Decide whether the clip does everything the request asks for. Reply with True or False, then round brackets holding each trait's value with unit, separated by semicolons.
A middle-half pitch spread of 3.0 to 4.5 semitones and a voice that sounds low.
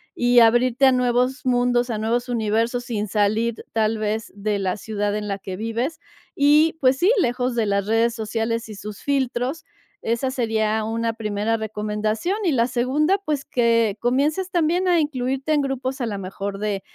False (3.3 semitones; 235 Hz)